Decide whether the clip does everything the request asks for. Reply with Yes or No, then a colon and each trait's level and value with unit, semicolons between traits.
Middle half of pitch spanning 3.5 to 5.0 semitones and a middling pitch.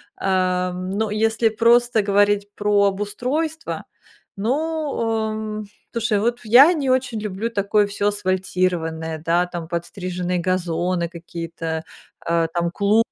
No: average, 3.8 semitones; high, 205 Hz